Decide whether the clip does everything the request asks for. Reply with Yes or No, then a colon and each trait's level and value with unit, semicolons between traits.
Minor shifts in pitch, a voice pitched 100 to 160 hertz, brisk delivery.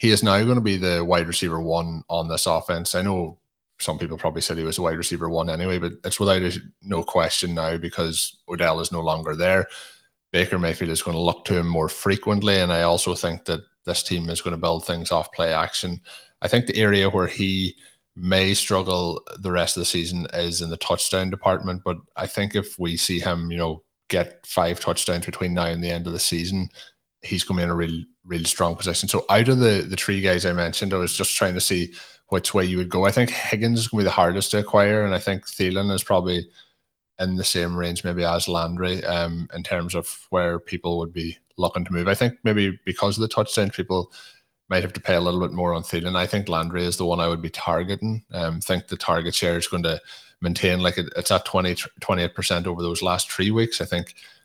No: narrow, 2.1 semitones; very low, 90 Hz; fast, 240 wpm